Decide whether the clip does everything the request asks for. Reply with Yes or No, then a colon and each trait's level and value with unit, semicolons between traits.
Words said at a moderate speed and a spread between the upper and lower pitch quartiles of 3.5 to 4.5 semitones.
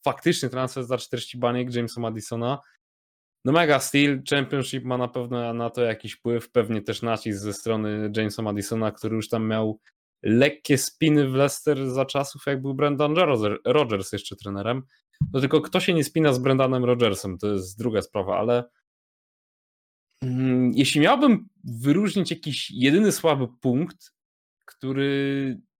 Yes: average, 150 wpm; average, 3.9 semitones